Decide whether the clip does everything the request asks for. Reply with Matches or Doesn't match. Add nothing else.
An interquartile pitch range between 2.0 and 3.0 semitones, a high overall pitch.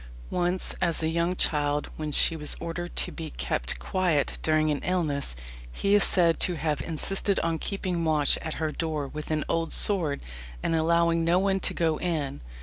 Doesn't match